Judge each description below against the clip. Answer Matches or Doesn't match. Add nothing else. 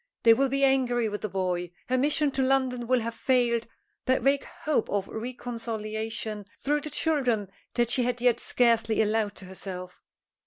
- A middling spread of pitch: Matches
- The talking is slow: Doesn't match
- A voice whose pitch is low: Doesn't match